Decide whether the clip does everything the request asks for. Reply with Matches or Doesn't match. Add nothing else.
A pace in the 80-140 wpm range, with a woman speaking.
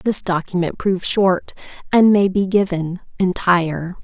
Matches